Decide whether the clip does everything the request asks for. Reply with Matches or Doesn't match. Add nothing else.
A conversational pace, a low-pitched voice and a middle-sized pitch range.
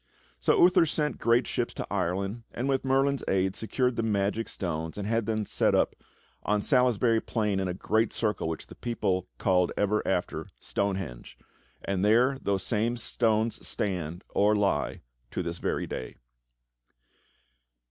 Matches